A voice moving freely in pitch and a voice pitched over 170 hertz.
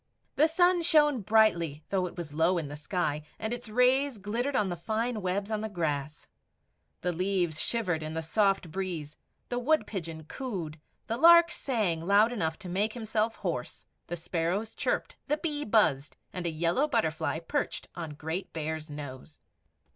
Yes: wide, 6.1 semitones; high, 190 Hz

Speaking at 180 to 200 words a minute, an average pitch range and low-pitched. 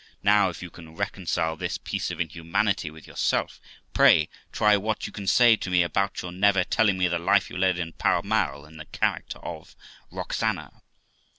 Yes: average, 190 wpm; average, 3.4 semitones; very low, 90 Hz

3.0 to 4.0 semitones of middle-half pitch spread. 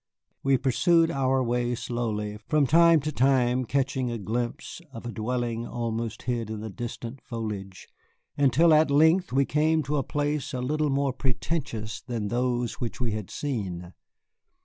Yes: average, 3.5 semitones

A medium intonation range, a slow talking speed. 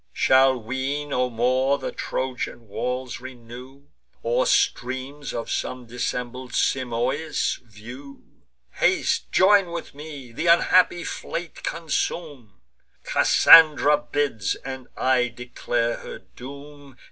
Yes: average, 3.0 semitones; slow, 105 wpm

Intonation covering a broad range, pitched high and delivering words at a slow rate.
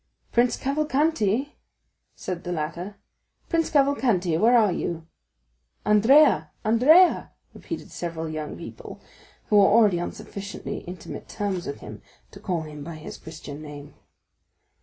Yes: wide, 7.2 semitones; high, 195 Hz; slow, 130 wpm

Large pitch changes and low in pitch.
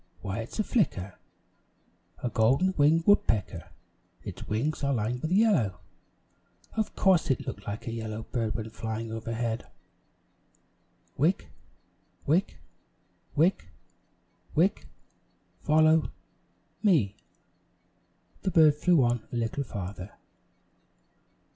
Yes: wide, 6.4 semitones; low, 120 Hz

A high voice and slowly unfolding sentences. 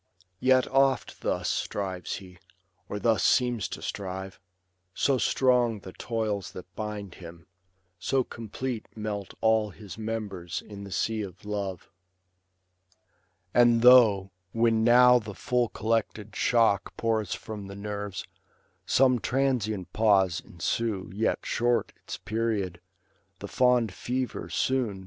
No: low, 110 Hz; slow, 125 wpm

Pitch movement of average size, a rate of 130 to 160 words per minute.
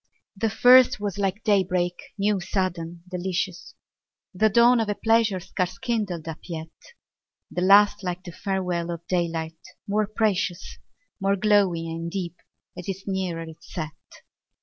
Yes: average, 3.1 semitones; average, 150 wpm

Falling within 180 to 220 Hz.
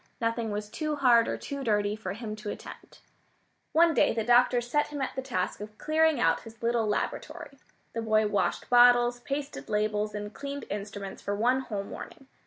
No: high, 230 Hz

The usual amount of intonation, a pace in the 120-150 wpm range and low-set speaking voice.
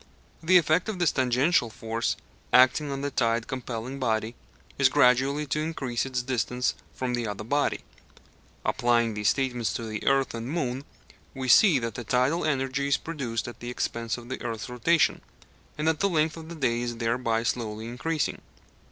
No: average, 3.6 semitones; average, 175 wpm; low, 125 Hz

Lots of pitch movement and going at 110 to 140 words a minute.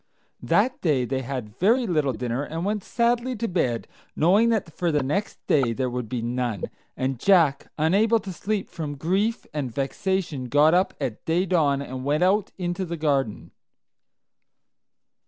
No: wide, 6.5 semitones; average, 165 wpm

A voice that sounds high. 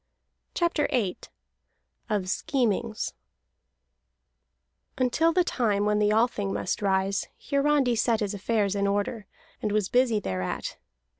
Yes: high, 215 Hz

